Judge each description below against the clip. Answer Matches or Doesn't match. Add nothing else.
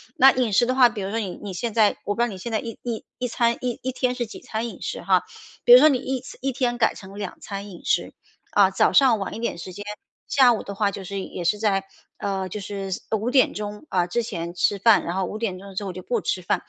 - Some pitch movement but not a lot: Matches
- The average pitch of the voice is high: Matches